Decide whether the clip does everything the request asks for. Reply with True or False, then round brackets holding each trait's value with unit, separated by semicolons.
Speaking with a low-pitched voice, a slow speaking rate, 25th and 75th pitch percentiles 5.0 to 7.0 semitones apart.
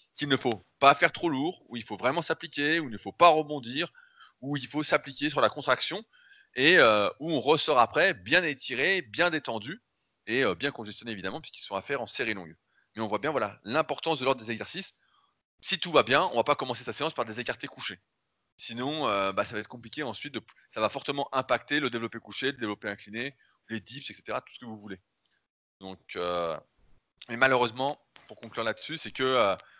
False (130 Hz; 220 wpm; 5.4 semitones)